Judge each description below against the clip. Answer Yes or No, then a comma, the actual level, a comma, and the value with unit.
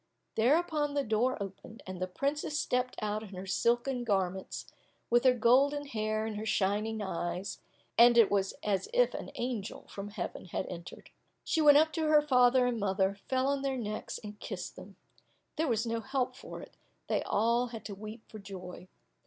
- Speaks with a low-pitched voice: No, high, 225 Hz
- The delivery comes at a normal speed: Yes, average, 185 wpm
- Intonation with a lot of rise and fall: No, average, 4.5 semitones